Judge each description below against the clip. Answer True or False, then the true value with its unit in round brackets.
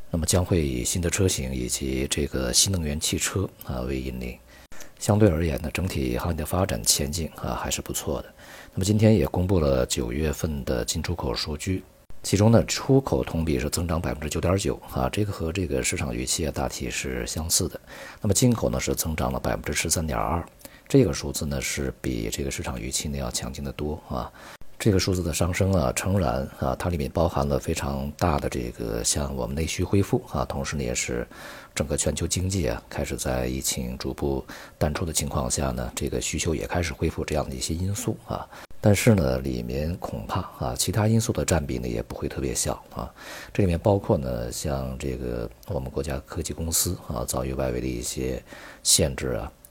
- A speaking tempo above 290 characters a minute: True (305 characters per minute)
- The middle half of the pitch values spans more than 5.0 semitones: True (5.4 semitones)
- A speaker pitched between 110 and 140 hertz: False (75 Hz)